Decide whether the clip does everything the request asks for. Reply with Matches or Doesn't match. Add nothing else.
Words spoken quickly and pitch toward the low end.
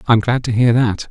Matches